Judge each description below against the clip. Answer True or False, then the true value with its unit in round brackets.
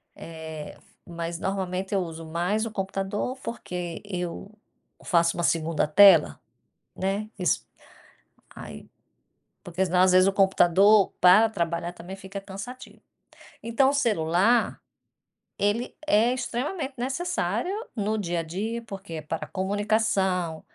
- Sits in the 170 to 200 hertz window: True (190 Hz)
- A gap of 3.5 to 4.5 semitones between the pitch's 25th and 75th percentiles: True (3.9 semitones)